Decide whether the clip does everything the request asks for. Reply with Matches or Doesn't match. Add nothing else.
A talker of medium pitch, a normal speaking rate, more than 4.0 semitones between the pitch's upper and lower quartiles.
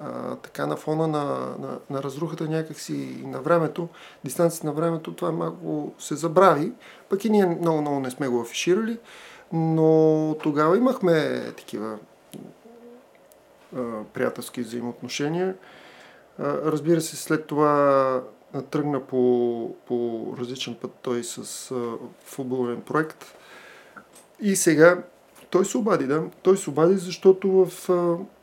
Matches